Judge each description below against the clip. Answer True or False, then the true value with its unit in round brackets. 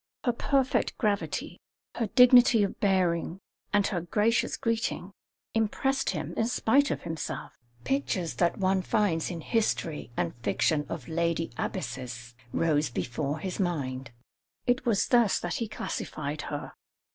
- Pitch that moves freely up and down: True (6.3 semitones)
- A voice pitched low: False (185 Hz)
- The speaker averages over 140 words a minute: False (135 wpm)